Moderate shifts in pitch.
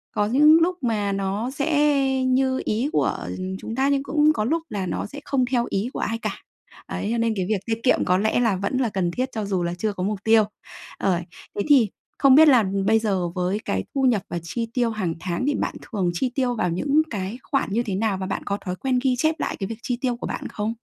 Yes: average, 4.8 semitones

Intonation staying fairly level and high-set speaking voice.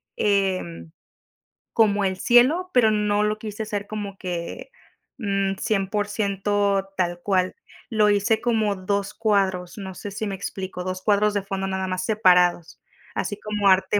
Yes: narrow, 2.0 semitones; high, 200 Hz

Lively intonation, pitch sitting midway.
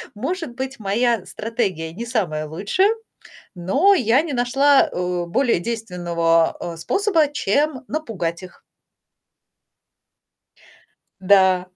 No: wide, 7.4 semitones; high, 220 Hz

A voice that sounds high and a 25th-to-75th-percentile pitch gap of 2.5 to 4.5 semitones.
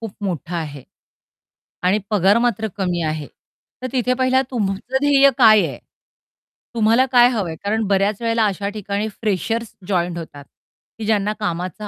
Yes: high, 210 Hz; average, 3.8 semitones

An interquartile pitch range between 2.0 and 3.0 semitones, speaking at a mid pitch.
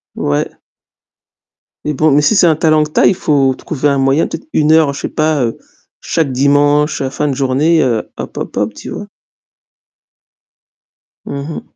Yes: narrow, 2.4 semitones; medium, 145 Hz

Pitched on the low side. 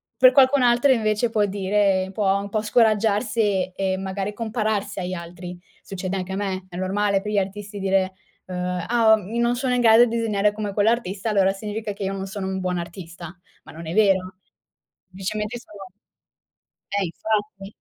No: high, 200 Hz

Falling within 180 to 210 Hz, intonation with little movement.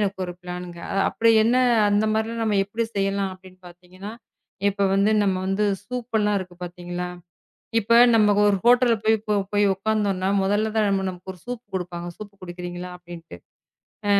No: high, 195 Hz; average, 3.2 semitones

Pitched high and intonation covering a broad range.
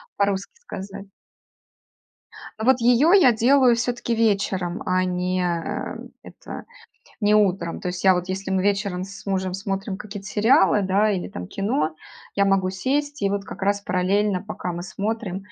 No: high, 195 Hz; narrow, 2.6 semitones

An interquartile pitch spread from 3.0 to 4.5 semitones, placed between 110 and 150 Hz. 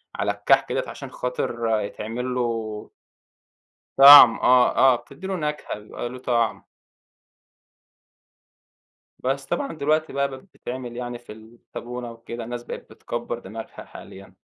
No: narrow, 2.6 semitones; low, 120 Hz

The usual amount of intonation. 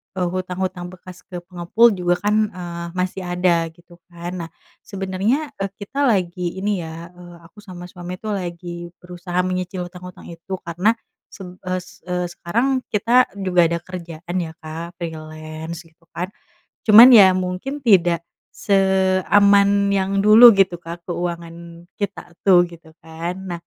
No: narrow, 1.9 semitones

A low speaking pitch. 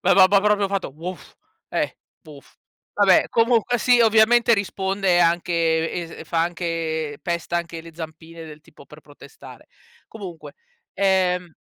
No: medium, 175 Hz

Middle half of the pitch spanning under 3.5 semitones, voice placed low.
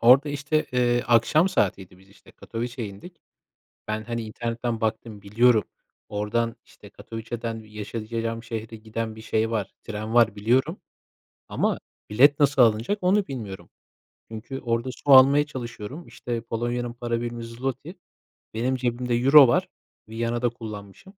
Yes: narrow, 2.4 semitones; low, 115 Hz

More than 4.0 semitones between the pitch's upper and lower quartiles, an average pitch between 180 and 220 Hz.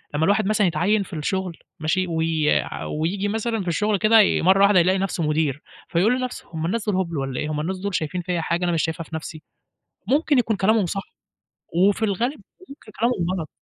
Yes: average, 4.5 semitones; medium, 185 Hz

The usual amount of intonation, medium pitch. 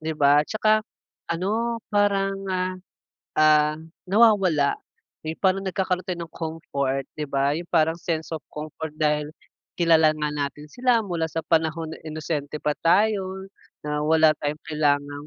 Yes: average, 3.7 semitones; medium, 160 Hz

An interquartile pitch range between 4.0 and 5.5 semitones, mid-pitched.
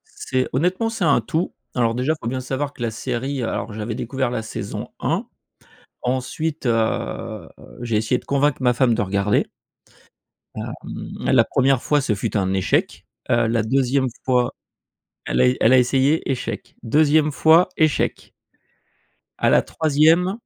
No: average, 4.3 semitones; low, 130 Hz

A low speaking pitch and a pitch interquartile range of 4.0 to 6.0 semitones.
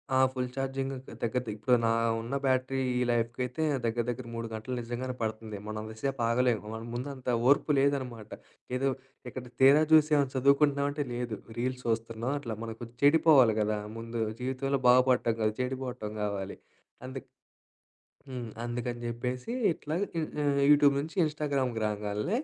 No: low, 125 Hz; average, 2.9 semitones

